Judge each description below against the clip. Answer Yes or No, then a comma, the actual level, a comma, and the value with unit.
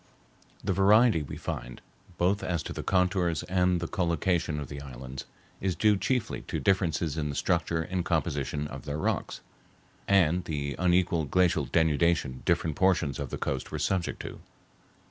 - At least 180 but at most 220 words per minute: No, average, 165 wpm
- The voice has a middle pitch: No, very low, 85 Hz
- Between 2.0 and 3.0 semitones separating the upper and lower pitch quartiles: No, average, 3.9 semitones